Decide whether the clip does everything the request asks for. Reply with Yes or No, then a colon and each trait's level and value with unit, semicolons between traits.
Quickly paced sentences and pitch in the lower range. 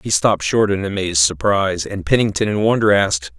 No: average, 195 wpm; low, 100 Hz